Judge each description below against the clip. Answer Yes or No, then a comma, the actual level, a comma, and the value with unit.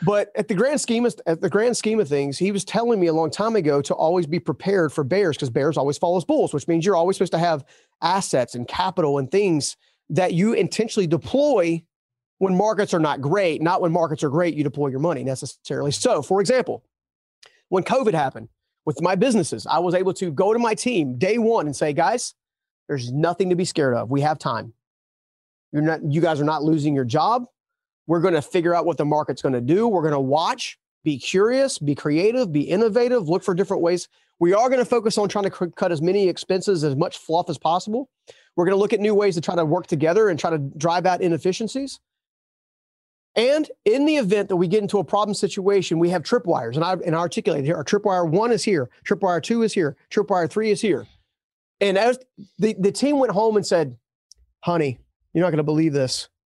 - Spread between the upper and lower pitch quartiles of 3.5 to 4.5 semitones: No, average, 5.0 semitones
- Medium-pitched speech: Yes, medium, 180 Hz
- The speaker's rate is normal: No, fast, 225 wpm